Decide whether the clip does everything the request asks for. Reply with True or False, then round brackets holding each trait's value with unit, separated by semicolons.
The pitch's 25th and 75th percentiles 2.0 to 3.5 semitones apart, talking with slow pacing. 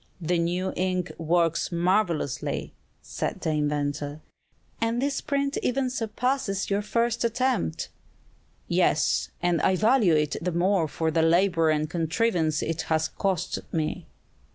False (5.1 semitones; 130 wpm)